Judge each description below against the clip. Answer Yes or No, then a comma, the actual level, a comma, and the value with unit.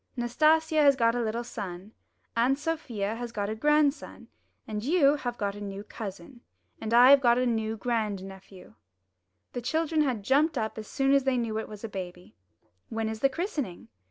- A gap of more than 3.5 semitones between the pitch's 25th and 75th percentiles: Yes, average, 4.6 semitones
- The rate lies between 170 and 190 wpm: Yes, average, 185 wpm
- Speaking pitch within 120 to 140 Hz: No, high, 235 Hz